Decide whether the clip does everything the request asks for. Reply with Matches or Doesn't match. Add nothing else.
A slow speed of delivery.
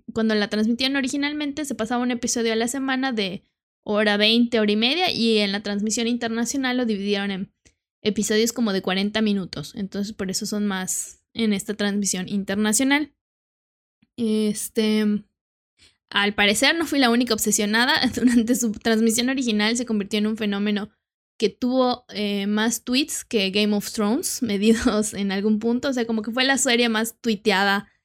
Doesn't match